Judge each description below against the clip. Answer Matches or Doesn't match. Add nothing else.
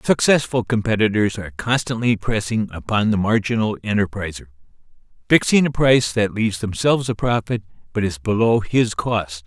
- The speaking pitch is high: Doesn't match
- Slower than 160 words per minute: Matches